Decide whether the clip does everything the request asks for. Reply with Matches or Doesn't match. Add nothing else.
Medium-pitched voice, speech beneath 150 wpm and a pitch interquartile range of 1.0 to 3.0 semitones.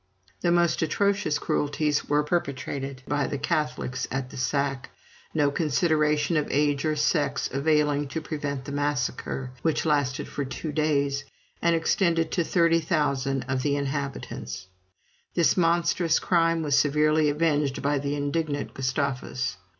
Matches